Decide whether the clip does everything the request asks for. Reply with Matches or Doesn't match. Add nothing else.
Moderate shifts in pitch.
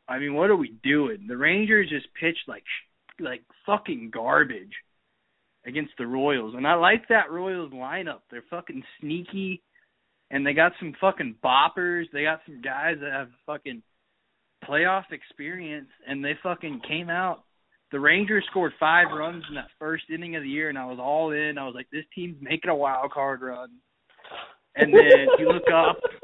Matches